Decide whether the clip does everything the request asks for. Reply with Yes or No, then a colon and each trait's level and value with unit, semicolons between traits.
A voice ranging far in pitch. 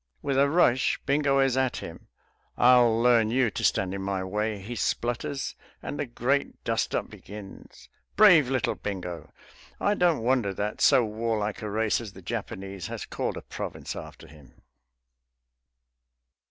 No: average, 4.7 semitones